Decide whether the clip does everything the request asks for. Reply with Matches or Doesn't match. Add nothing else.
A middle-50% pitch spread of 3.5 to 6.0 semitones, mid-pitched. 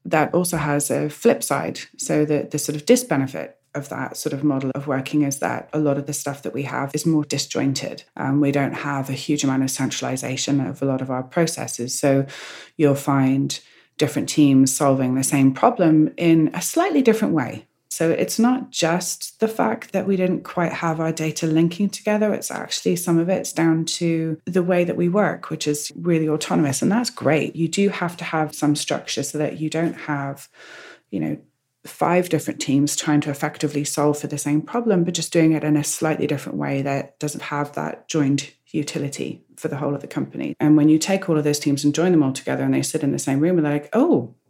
Doesn't match